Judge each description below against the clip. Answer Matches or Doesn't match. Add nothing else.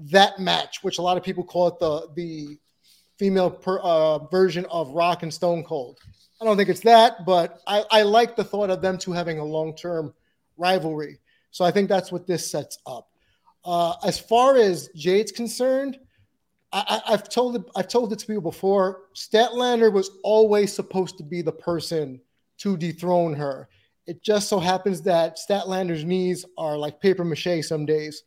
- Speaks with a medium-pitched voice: Matches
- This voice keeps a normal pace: Matches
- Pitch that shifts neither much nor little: Matches